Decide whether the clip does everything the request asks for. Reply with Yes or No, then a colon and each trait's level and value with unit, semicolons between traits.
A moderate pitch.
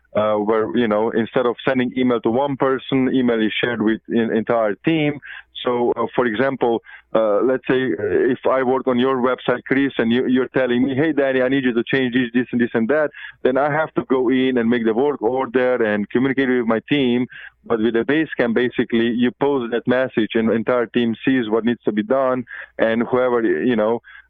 No: low, 125 Hz